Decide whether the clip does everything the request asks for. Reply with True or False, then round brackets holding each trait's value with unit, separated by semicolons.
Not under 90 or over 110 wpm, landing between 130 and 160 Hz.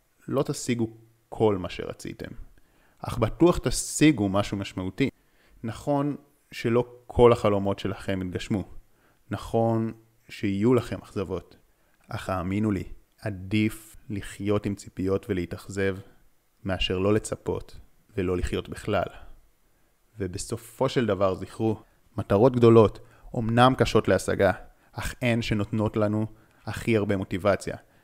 False (105 wpm; 110 Hz)